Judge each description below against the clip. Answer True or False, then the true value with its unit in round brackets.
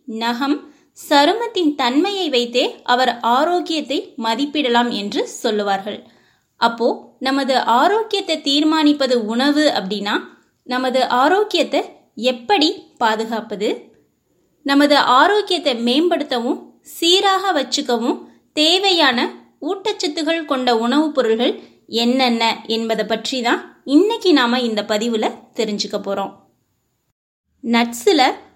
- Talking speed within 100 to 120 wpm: False (85 wpm)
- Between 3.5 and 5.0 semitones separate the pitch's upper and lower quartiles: False (5.4 semitones)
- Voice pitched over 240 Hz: True (270 Hz)